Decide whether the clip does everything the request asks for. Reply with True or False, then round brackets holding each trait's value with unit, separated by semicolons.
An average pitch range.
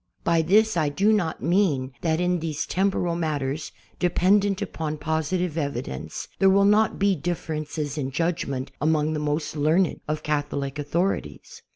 True (3.4 semitones)